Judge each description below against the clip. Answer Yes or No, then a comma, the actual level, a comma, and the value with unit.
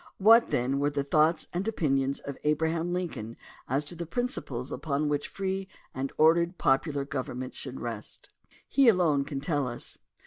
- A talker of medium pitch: Yes, medium, 150 Hz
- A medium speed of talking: Yes, average, 165 wpm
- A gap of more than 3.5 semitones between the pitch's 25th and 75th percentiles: Yes, average, 4.1 semitones